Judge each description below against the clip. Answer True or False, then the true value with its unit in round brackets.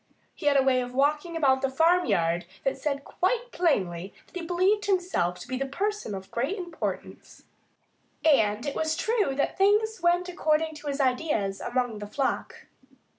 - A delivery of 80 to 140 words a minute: False (175 wpm)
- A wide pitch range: True (6.1 semitones)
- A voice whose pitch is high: True (290 Hz)